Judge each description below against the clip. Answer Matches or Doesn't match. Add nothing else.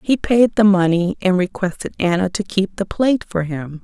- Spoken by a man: Doesn't match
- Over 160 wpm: Matches